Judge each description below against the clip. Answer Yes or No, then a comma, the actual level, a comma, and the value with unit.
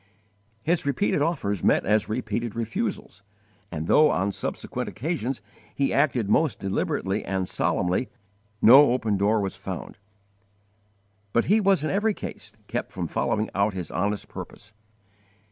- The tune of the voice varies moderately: No, wide, 6.1 semitones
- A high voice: No, low, 110 Hz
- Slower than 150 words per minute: Yes, average, 140 wpm